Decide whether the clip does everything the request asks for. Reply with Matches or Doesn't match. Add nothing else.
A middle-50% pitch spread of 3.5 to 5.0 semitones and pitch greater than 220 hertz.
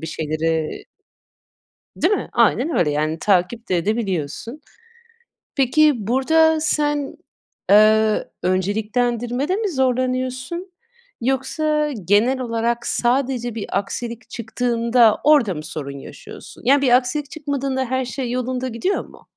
Matches